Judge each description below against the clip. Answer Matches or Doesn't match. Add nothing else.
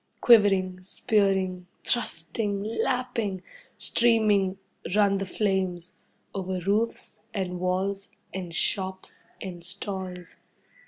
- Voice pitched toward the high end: Matches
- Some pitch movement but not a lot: Doesn't match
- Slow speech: Matches